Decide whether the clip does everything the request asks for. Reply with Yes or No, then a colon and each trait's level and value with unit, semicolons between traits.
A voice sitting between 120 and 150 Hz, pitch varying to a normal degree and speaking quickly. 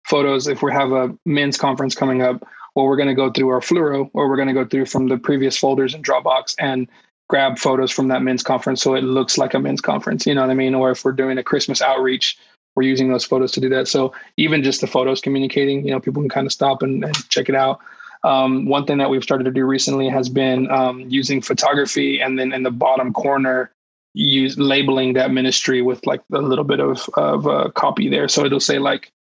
No: low, 135 Hz; narrow, 0.8 semitones; fast, 240 wpm